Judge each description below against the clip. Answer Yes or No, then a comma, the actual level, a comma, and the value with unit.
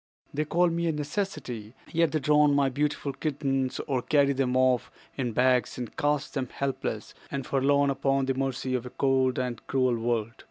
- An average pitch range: No, narrow, 2.3 semitones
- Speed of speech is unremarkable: Yes, average, 185 wpm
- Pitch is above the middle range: No, low, 135 Hz